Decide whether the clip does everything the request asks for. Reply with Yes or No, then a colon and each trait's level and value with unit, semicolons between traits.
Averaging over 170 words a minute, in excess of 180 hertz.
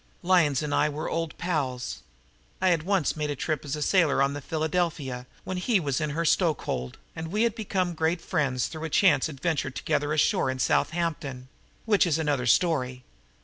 No: average, 185 wpm; medium, 155 Hz